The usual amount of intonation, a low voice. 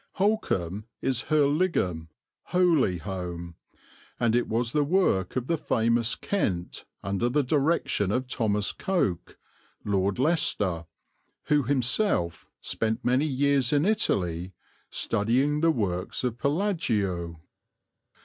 No: wide, 7.6 semitones; low, 120 Hz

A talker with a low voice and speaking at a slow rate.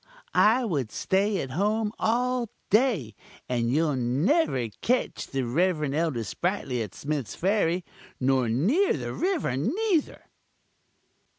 No: medium, 170 Hz; slow, 120 wpm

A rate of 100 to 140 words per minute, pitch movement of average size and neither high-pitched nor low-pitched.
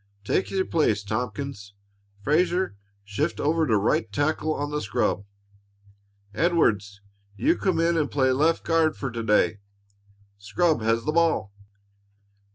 No: slow, 135 wpm; wide, 7.3 semitones; medium, 145 Hz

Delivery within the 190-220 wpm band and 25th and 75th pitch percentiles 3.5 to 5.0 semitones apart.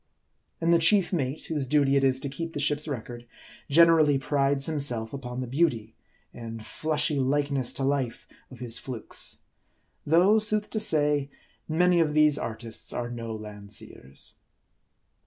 No: average, 150 wpm; average, 4.4 semitones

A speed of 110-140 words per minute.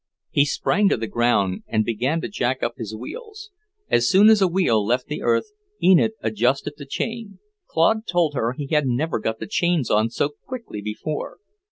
No: average, 190 wpm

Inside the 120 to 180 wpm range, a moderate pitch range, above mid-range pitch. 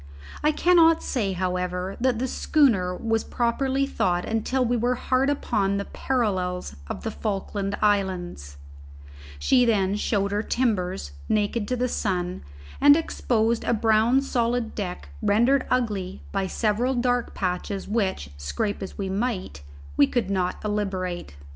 Yes: average, 140 wpm; average, 4.6 semitones; high, 210 Hz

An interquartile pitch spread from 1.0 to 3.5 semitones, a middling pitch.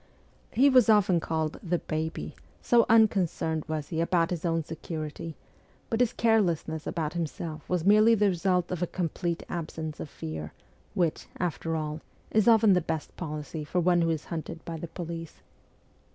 Yes: average, 2.7 semitones; medium, 170 Hz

